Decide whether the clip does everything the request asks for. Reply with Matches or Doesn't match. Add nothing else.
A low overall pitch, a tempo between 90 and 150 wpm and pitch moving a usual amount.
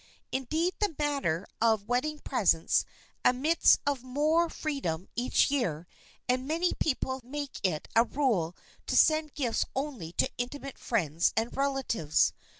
Doesn't match